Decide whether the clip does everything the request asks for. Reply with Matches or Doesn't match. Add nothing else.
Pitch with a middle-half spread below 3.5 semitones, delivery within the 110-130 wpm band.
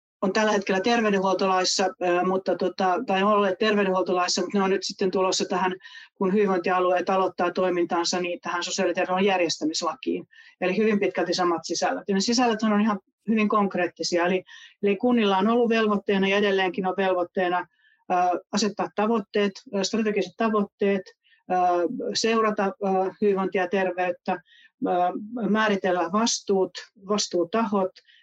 Matches